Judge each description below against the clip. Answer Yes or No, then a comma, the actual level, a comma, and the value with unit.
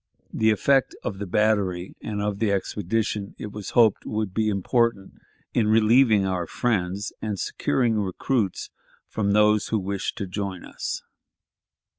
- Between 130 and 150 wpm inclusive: Yes, average, 145 wpm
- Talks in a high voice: No, low, 105 Hz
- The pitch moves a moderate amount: No, narrow, 2.1 semitones